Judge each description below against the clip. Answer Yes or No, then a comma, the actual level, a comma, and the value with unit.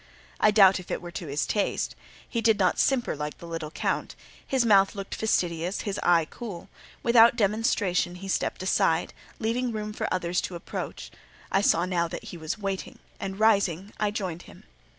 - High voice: Yes, high, 195 Hz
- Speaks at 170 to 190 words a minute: Yes, average, 185 wpm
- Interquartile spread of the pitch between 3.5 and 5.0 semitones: Yes, average, 3.8 semitones